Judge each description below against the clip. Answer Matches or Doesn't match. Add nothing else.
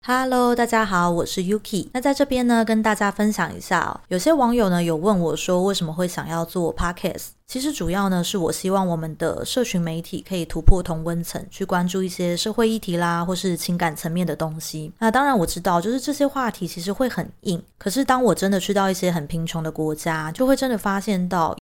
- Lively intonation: Doesn't match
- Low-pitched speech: Doesn't match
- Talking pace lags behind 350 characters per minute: Doesn't match